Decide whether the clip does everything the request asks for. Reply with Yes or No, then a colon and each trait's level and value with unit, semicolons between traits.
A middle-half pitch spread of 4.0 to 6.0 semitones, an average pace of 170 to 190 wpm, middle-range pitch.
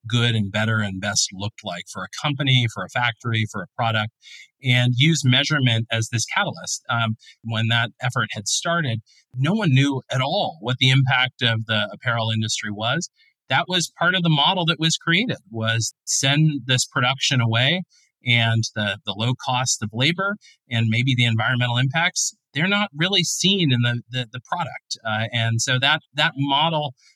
No: average, 4.6 semitones; average, 180 wpm; low, 125 Hz